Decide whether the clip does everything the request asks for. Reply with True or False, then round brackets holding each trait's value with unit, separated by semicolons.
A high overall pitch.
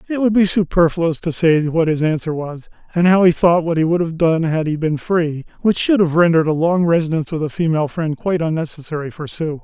False (165 Hz)